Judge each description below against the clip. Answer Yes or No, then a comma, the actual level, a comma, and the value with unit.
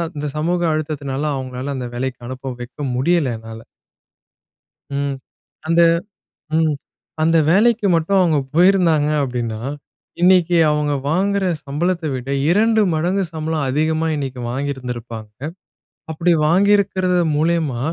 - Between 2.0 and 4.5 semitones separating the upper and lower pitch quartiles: No, average, 5.0 semitones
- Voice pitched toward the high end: No, medium, 155 Hz